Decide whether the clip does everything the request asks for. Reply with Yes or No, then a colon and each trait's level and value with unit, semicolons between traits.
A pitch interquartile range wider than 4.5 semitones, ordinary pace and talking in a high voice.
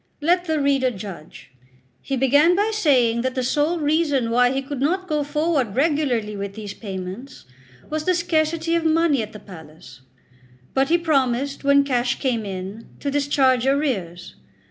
Yes: average, 5.2 semitones; average, 165 wpm; very high, 275 Hz